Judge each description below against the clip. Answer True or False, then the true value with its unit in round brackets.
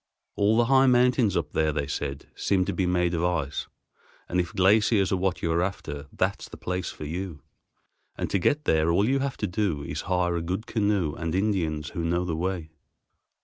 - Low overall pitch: True (90 Hz)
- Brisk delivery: True (215 wpm)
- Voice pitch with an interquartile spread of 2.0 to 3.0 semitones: False (3.7 semitones)